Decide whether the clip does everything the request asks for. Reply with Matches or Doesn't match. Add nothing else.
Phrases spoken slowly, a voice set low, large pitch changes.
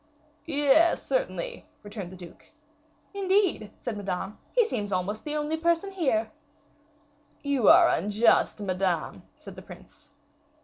Doesn't match